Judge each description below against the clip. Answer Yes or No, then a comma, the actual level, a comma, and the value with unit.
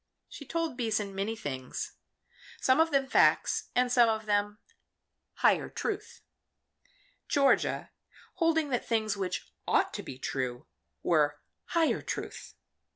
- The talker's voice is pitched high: Yes, high, 225 Hz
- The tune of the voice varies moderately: No, wide, 6.4 semitones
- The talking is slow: Yes, slow, 125 wpm